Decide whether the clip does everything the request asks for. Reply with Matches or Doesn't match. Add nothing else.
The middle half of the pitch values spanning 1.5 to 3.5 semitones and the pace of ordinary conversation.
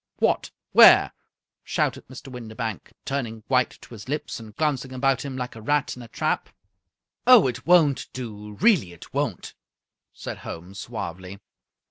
Doesn't match